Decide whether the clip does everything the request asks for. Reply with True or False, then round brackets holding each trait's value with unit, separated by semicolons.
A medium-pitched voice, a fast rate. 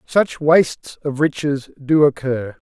False (145 Hz; 135 wpm)